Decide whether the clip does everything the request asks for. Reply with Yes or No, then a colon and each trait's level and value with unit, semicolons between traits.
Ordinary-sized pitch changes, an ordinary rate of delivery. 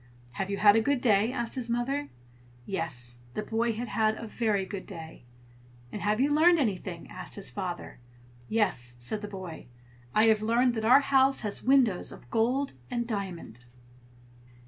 Yes: average, 4.1 semitones; average, 170 wpm